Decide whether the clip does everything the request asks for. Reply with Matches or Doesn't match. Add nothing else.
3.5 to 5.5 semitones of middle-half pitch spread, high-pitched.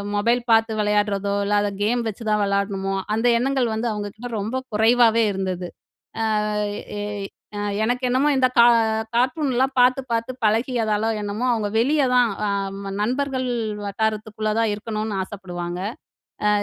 Doesn't match